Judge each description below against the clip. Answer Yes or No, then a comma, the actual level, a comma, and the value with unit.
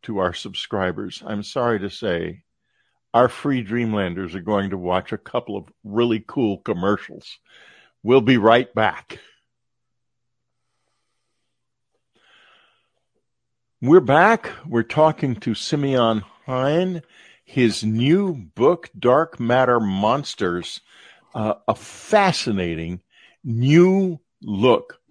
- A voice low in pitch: Yes, low, 120 Hz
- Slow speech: Yes, slow, 100 wpm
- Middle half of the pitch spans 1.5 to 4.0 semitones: No, average, 4.5 semitones